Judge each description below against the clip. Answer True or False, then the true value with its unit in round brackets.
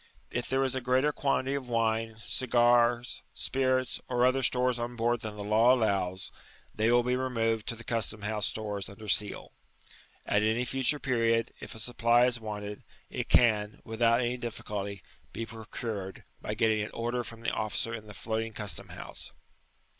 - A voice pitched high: False (115 Hz)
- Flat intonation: True (2.2 semitones)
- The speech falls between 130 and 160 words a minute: False (175 wpm)